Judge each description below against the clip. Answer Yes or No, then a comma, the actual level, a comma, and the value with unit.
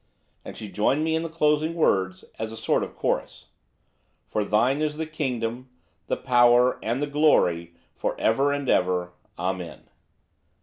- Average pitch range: No, wide, 6.5 semitones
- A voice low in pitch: Yes, low, 125 Hz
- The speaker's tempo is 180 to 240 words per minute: No, average, 160 wpm